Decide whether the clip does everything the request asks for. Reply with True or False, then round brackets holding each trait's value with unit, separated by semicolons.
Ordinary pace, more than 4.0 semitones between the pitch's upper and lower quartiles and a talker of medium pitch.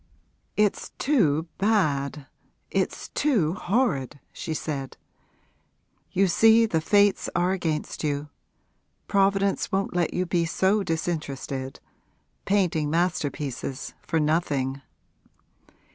False (100 wpm; 5.0 semitones; 170 Hz)